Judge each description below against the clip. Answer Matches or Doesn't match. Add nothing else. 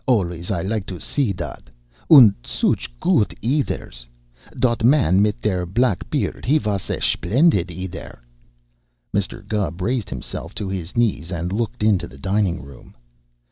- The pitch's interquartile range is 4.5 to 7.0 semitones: Matches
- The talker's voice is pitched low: Matches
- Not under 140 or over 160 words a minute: Matches